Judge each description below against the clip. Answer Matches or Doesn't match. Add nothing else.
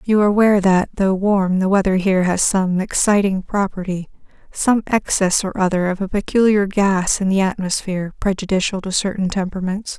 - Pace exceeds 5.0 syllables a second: Matches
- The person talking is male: Doesn't match